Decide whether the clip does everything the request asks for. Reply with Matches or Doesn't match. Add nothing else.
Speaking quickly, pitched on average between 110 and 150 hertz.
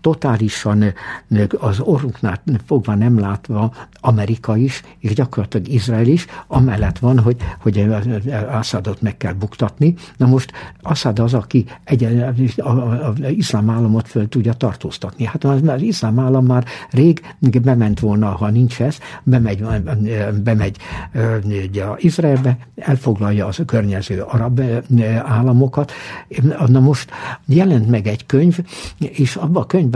Doesn't match